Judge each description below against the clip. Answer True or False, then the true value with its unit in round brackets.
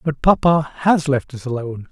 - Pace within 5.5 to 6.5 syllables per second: False (5.0 syllables/s)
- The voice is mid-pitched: True (145 Hz)